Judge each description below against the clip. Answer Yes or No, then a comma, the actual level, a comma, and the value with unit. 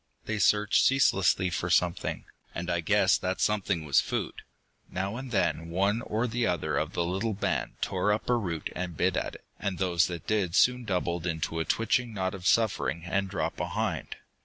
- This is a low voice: Yes, very low, 95 Hz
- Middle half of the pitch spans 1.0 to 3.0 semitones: No, average, 3.6 semitones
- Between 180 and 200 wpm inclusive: Yes, average, 195 wpm